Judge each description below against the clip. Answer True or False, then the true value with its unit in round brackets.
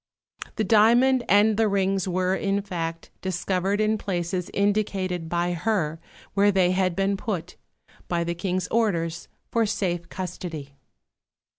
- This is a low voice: False (190 Hz)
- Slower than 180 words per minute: True (135 wpm)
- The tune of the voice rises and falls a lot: False (2.8 semitones)